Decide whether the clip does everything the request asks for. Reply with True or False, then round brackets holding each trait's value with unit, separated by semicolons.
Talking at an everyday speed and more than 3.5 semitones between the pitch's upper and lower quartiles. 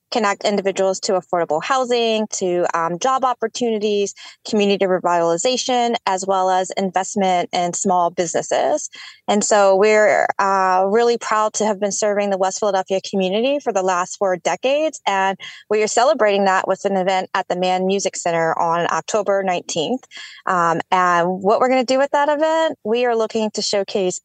True (170 wpm; 4.1 semitones)